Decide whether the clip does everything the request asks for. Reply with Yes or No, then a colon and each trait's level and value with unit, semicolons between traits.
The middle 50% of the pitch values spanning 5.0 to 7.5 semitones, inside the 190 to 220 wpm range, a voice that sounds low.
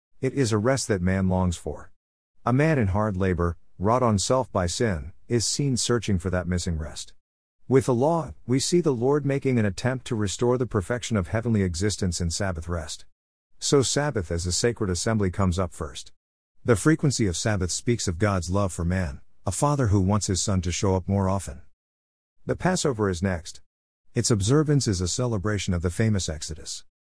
Yes: wide, 5.4 semitones; average, 195 wpm; low, 100 Hz